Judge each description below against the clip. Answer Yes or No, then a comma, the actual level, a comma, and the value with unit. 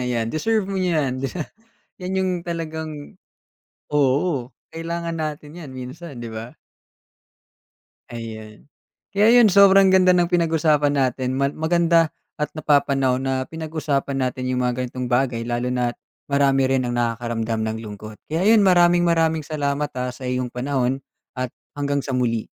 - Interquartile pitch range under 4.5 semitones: No, average, 4.8 semitones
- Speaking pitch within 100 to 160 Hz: Yes, medium, 140 Hz